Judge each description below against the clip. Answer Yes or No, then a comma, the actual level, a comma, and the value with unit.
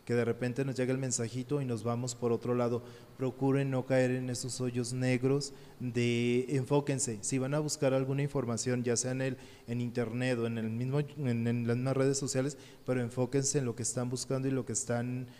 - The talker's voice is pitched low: Yes, low, 125 Hz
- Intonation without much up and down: Yes, narrow, 1.8 semitones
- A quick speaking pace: Yes, fast, 215 wpm